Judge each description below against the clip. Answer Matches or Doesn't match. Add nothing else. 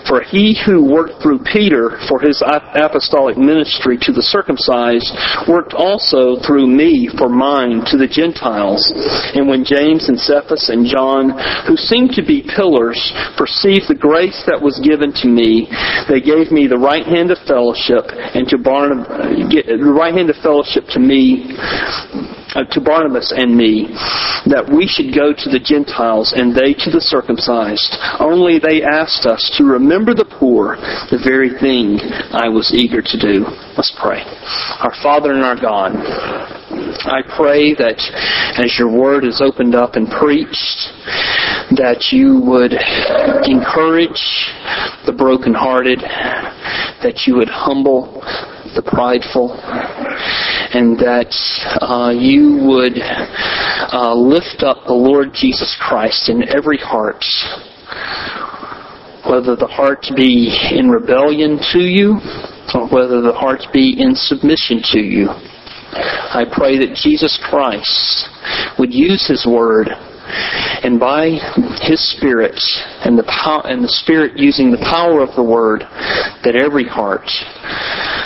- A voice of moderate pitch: Matches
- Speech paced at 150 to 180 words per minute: Doesn't match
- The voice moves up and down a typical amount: Doesn't match